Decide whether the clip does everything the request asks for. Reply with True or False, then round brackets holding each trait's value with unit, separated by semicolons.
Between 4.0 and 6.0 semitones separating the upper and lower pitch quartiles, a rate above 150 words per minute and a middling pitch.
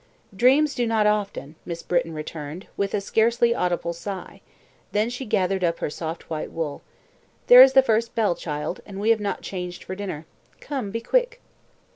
False (5.3 semitones; 180 wpm; 200 Hz)